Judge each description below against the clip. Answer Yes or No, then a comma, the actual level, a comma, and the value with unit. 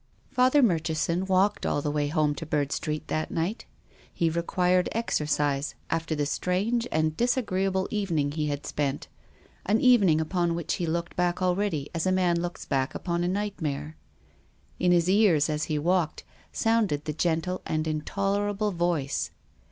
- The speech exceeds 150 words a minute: Yes, average, 165 wpm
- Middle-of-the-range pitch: Yes, medium, 170 Hz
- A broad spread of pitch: No, average, 3.8 semitones